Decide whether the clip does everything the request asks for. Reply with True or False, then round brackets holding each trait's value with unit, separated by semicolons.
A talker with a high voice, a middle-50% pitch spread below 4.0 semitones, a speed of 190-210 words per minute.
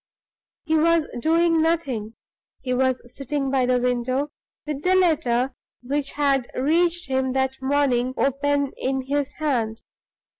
False (275 Hz; 2.8 semitones; 135 wpm)